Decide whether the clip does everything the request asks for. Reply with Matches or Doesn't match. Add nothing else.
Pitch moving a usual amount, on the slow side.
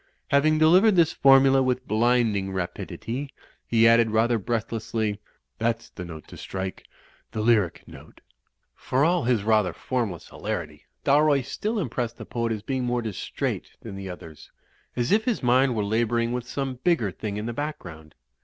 Doesn't match